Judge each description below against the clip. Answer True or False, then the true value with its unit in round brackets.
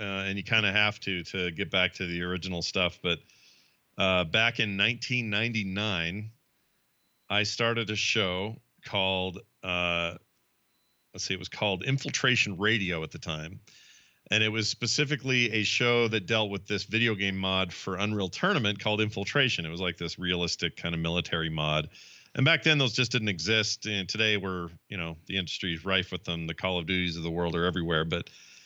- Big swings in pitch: False (3.9 semitones)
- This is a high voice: False (95 Hz)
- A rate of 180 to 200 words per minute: True (190 wpm)